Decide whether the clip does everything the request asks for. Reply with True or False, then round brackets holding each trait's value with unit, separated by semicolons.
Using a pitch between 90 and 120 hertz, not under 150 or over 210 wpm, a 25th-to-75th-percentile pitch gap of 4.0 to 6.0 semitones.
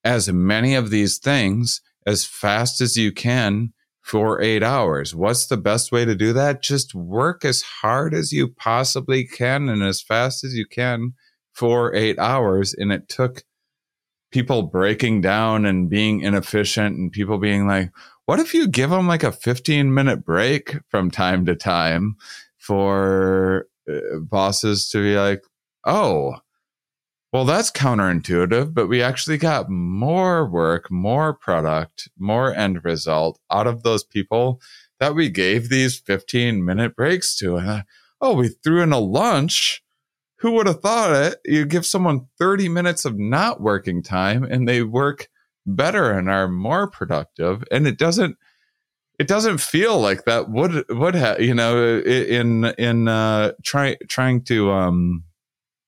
True (115 Hz; 155 wpm; 5.2 semitones)